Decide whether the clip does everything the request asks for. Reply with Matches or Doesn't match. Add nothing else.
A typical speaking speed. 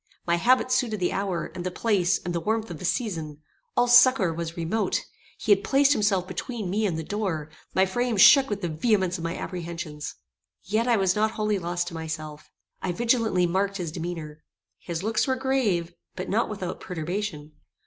Matches